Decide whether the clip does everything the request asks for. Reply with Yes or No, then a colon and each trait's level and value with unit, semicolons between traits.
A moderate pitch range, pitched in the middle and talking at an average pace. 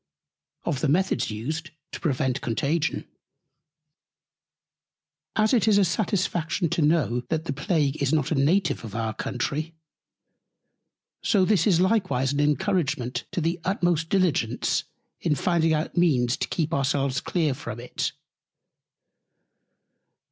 No: average, 4.4 semitones; medium, 155 Hz; slow, 130 wpm